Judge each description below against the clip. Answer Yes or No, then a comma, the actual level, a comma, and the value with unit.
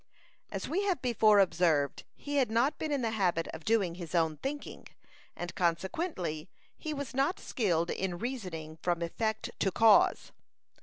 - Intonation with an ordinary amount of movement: No, wide, 7.2 semitones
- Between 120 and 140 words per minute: No, average, 160 wpm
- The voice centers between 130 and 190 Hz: No, high, 200 Hz